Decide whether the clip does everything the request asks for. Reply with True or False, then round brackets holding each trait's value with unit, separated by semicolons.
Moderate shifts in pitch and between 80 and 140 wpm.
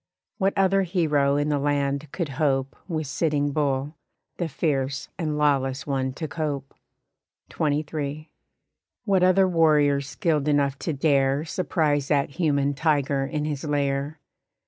False (2.1 semitones; 135 wpm)